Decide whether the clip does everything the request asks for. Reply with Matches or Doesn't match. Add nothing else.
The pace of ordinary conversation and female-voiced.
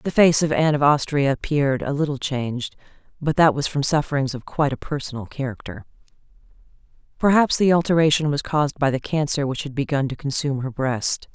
Matches